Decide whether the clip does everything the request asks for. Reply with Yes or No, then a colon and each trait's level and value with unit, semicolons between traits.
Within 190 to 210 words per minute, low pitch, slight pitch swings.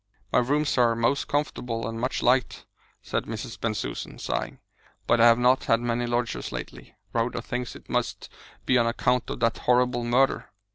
No: average, 175 wpm; low, 120 Hz; narrow, 1.3 semitones